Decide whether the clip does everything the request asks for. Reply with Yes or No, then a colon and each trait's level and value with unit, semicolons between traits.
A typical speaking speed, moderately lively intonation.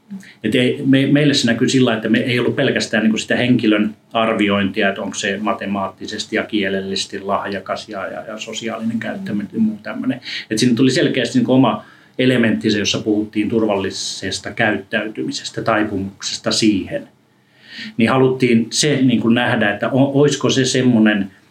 Yes: average, 145 wpm; average, 3.6 semitones